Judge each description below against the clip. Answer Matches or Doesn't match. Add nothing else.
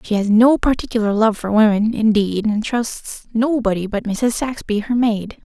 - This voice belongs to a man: Doesn't match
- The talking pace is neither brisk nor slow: Matches